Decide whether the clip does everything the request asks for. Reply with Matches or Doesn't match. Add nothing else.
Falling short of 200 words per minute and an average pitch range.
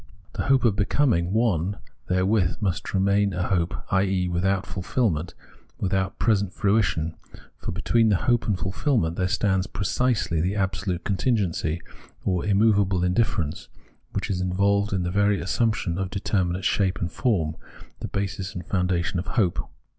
Doesn't match